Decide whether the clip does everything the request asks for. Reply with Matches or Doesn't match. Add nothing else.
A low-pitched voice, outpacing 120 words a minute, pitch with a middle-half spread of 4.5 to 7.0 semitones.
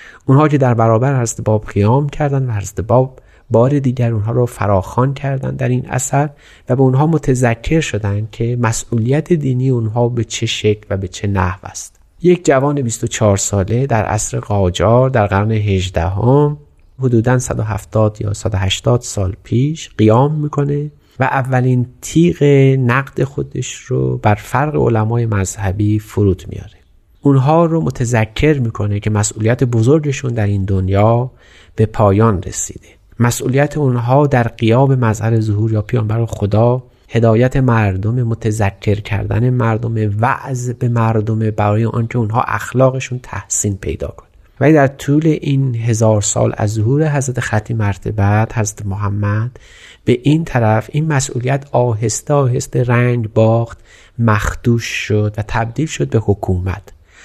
Doesn't match